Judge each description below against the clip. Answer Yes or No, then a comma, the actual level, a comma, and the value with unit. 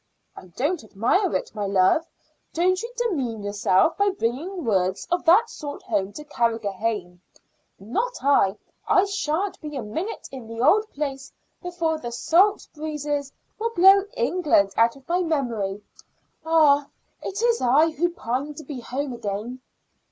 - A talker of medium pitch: No, very high, 285 Hz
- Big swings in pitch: Yes, wide, 7.6 semitones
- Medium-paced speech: Yes, average, 150 wpm